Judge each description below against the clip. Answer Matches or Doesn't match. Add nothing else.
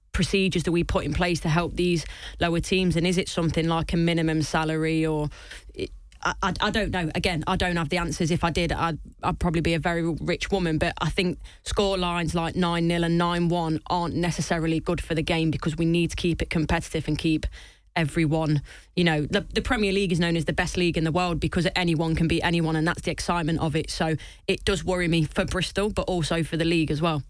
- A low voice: Doesn't match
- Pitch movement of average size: Doesn't match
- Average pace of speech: Doesn't match